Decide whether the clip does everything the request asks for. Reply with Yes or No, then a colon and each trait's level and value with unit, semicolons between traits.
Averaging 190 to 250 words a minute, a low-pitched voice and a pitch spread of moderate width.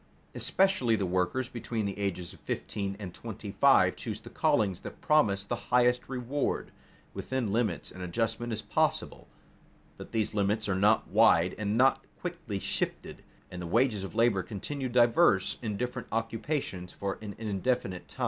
No: average, 160 wpm; low, 110 Hz; average, 4.0 semitones